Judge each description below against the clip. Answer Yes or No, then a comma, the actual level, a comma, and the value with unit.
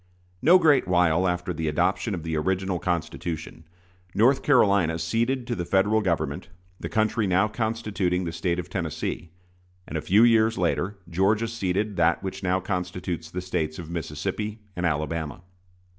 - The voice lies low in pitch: Yes, very low, 90 Hz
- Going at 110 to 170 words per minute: Yes, average, 160 wpm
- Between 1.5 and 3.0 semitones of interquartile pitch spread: No, average, 4.0 semitones